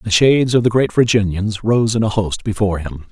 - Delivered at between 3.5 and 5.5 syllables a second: No, 5.7 syllables/s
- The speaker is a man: Yes, male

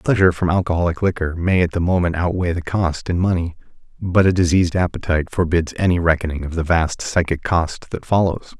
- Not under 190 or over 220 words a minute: Yes, average, 195 wpm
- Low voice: Yes, very low, 85 Hz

